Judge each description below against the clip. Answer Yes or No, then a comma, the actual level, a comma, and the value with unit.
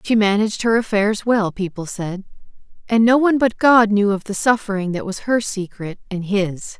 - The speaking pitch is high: Yes, high, 205 Hz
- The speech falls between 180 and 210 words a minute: Yes, average, 195 wpm